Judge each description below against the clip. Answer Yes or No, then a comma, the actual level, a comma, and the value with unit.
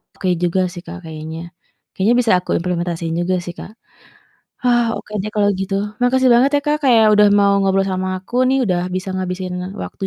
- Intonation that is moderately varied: Yes, average, 4.2 semitones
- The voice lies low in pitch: No, high, 190 Hz